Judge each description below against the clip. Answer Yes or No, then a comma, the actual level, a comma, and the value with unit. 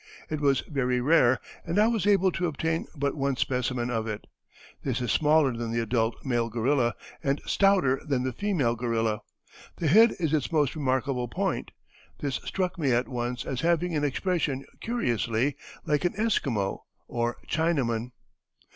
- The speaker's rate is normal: Yes, average, 165 wpm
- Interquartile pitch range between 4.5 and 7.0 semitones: Yes, average, 5.2 semitones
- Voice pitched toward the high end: No, low, 135 Hz